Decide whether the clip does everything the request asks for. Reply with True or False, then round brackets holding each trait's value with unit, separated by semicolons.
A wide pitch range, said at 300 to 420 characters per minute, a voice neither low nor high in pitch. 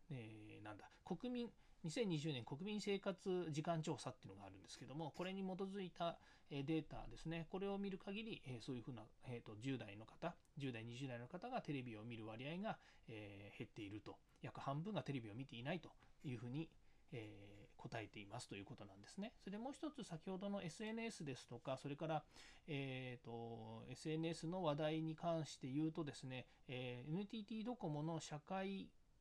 True (6.7 semitones; 345 characters per minute; 150 Hz)